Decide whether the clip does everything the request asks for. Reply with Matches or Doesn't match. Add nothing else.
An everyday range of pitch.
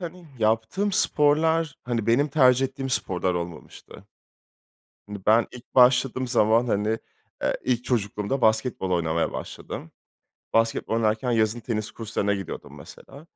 Matches